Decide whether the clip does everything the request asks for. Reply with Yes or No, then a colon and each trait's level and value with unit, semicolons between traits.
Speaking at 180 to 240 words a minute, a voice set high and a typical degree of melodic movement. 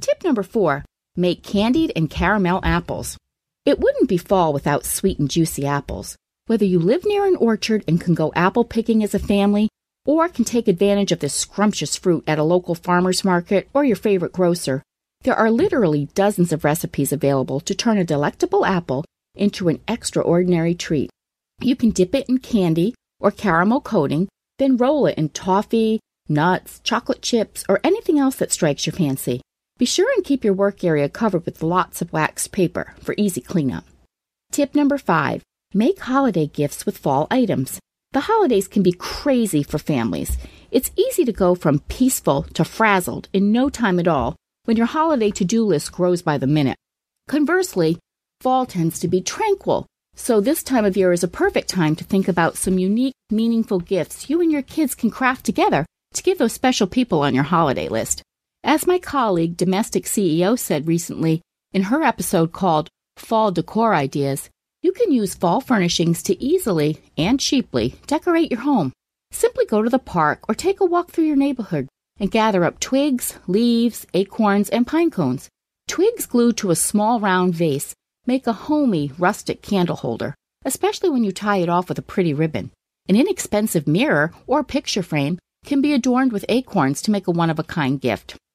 No: average, 185 wpm; high, 200 Hz; wide, 7.3 semitones